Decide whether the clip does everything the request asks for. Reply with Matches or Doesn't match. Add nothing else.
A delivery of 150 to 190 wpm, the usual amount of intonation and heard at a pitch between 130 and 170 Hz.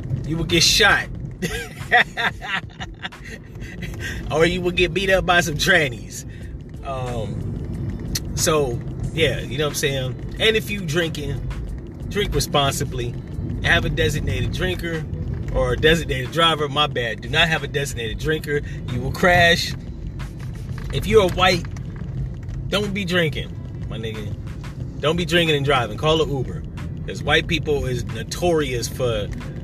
Doesn't match